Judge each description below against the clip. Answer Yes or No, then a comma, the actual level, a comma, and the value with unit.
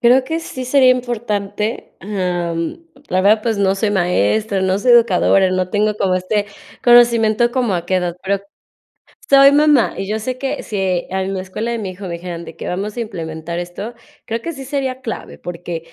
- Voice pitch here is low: No, high, 205 Hz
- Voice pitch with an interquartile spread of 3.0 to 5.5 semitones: Yes, average, 4.5 semitones